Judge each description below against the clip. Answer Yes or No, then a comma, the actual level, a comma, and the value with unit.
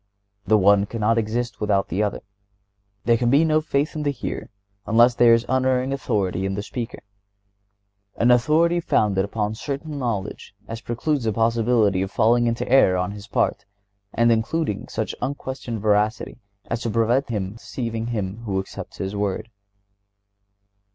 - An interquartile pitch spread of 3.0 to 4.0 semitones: Yes, average, 3.3 semitones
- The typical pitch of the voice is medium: No, low, 115 Hz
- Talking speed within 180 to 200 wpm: No, average, 160 wpm